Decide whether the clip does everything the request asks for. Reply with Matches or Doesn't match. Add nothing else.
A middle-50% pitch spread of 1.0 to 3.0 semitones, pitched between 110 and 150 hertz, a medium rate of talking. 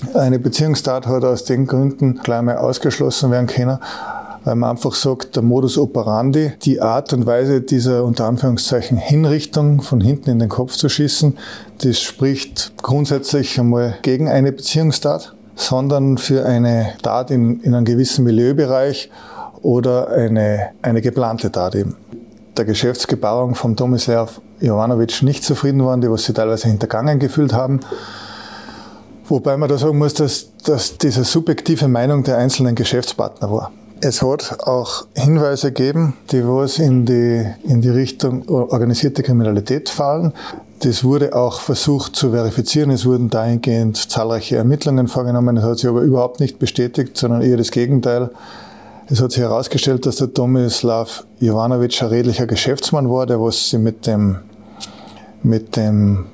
Matches